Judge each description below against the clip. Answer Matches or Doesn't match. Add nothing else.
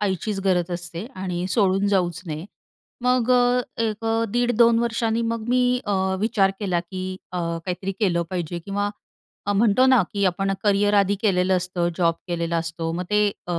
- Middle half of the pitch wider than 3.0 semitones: Matches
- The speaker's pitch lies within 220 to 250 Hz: Doesn't match